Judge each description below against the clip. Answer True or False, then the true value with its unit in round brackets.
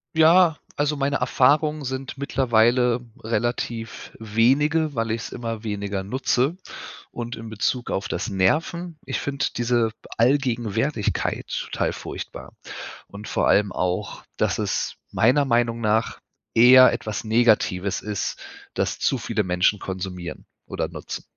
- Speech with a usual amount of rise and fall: True (4.1 semitones)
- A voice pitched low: True (120 Hz)